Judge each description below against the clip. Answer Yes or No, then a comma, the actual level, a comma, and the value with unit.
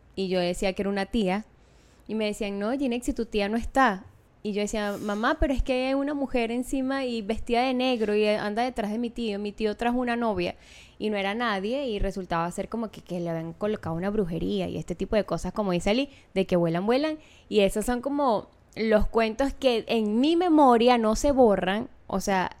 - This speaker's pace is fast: Yes, fast, 225 wpm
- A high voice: Yes, high, 215 Hz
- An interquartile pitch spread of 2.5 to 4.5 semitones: Yes, average, 3.8 semitones